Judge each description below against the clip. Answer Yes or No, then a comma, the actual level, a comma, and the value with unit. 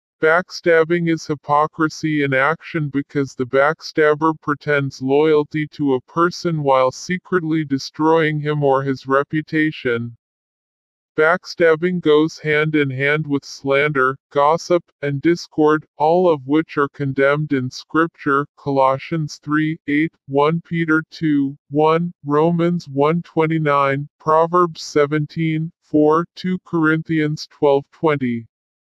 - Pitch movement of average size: No, narrow, 2.3 semitones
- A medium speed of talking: No, slow, 110 wpm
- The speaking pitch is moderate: Yes, medium, 150 Hz